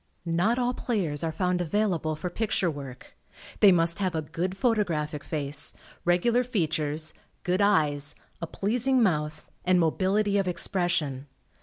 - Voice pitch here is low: No, medium, 175 Hz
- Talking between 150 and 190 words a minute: No, average, 140 wpm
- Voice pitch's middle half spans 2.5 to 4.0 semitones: No, average, 4.6 semitones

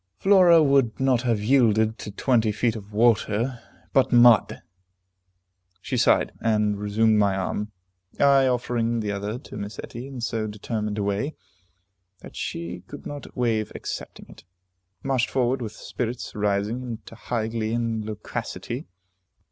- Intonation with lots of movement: No, average, 2.8 semitones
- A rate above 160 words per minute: No, average, 145 wpm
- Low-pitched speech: Yes, low, 115 Hz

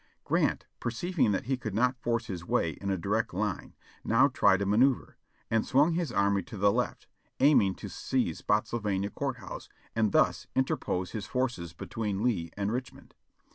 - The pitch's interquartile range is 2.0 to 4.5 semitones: Yes, average, 4.2 semitones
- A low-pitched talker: Yes, low, 110 Hz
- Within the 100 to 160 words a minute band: No, average, 175 wpm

